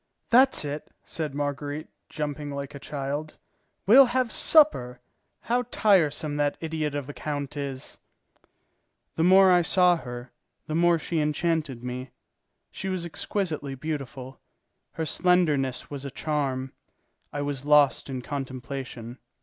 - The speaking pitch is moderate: Yes, medium, 145 Hz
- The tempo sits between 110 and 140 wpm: Yes, slow, 135 wpm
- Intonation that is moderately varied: Yes, average, 3.6 semitones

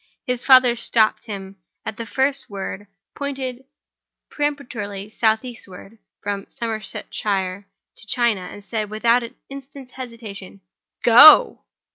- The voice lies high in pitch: Yes, high, 225 Hz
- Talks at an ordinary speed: No, slow, 110 wpm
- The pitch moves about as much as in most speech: Yes, average, 3.8 semitones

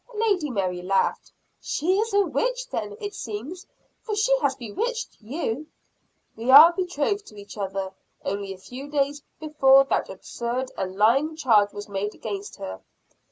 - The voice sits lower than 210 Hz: No, very high, 270 Hz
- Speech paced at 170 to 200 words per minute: No, average, 160 wpm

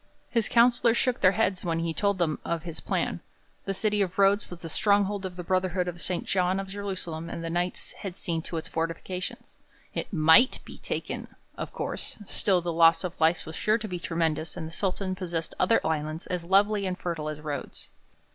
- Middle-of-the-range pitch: Yes, medium, 180 Hz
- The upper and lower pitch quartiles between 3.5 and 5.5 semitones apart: No, average, 3.0 semitones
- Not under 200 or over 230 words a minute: Yes, fast, 205 wpm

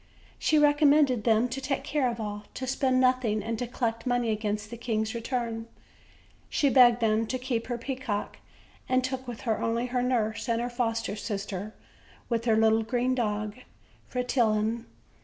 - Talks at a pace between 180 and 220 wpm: No, average, 170 wpm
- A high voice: Yes, high, 235 Hz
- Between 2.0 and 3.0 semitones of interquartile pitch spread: Yes, narrow, 2.6 semitones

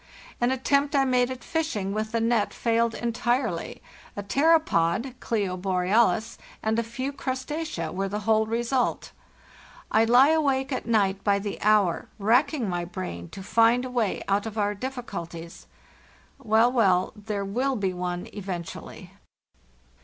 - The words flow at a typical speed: Yes, average, 145 wpm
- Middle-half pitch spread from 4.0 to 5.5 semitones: Yes, average, 4.3 semitones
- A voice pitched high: Yes, high, 225 Hz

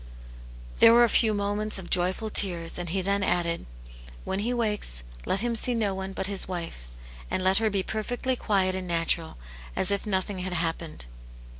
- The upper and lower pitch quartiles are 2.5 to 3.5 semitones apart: Yes, average, 3.1 semitones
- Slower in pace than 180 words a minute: No, average, 185 wpm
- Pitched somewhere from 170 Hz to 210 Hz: Yes, high, 190 Hz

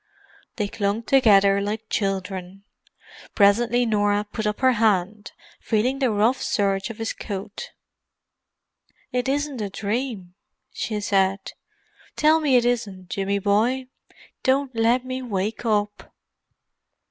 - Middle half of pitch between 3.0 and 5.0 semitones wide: Yes, average, 3.6 semitones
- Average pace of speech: No, slow, 125 wpm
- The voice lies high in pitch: Yes, high, 215 Hz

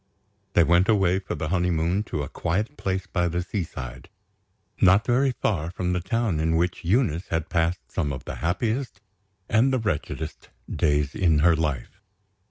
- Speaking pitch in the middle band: No, very low, 90 Hz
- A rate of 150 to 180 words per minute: Yes, average, 170 wpm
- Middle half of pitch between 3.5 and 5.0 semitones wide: Yes, average, 3.8 semitones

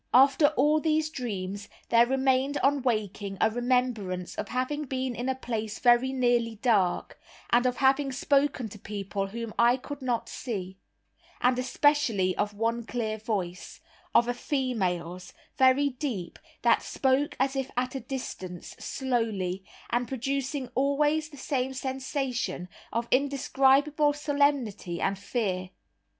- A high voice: Yes, very high, 250 Hz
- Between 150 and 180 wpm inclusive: No, slow, 135 wpm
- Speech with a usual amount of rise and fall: Yes, average, 4.1 semitones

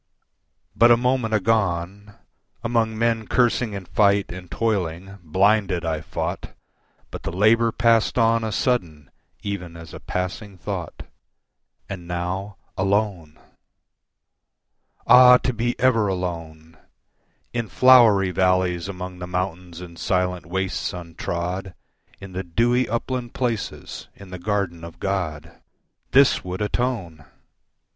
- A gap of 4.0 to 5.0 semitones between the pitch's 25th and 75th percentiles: Yes, average, 4.3 semitones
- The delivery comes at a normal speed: No, slow, 120 wpm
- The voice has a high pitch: No, very low, 95 Hz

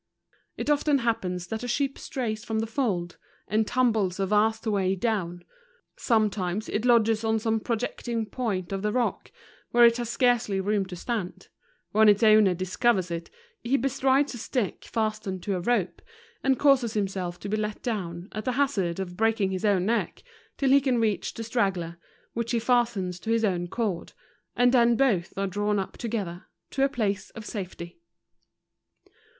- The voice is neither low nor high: No, high, 215 Hz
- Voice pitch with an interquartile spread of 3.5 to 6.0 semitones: Yes, average, 3.8 semitones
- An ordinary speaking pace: Yes, average, 180 wpm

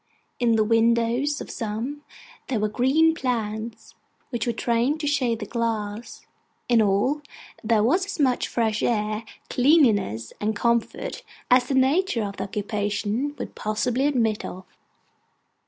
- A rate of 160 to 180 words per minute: No, average, 140 wpm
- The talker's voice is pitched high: Yes, high, 230 Hz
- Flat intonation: No, average, 3.7 semitones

